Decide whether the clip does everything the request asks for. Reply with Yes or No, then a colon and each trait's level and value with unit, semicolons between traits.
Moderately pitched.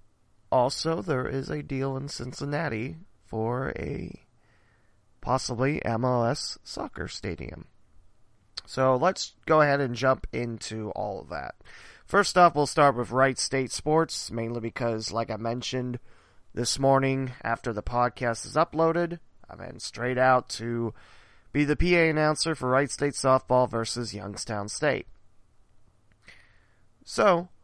No: low, 120 Hz